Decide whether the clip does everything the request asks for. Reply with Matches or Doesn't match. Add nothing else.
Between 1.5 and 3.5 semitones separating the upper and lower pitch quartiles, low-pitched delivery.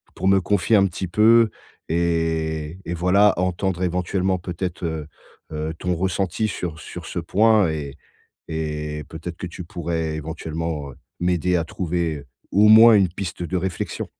Matches